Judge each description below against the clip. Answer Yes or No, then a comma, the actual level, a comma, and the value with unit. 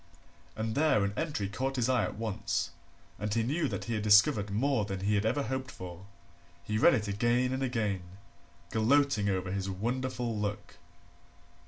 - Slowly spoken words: No, average, 175 wpm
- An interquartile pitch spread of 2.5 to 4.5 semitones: Yes, average, 4.2 semitones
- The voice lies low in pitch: Yes, low, 110 Hz